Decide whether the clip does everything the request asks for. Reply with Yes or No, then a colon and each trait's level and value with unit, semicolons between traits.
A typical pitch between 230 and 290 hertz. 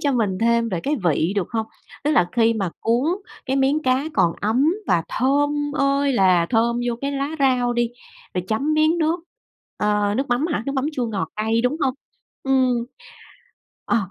Yes: high, 245 Hz